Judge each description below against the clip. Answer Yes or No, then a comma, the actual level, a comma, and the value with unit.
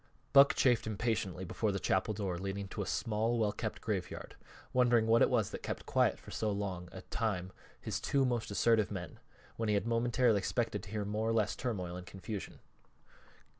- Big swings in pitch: No, average, 2.9 semitones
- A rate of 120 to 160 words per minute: No, average, 195 wpm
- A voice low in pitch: Yes, low, 105 Hz